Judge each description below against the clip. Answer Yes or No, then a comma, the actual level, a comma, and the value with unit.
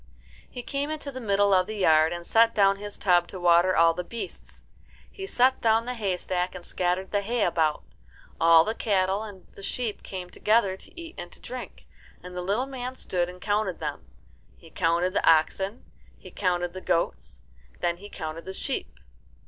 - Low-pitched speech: No, high, 190 Hz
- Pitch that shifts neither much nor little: Yes, average, 4.1 semitones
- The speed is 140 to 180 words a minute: No, average, 195 wpm